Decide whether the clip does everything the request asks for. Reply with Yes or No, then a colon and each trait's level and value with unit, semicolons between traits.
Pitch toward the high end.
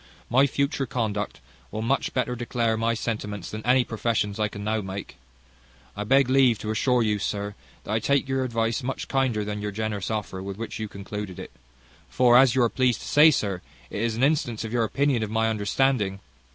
No: low, 115 Hz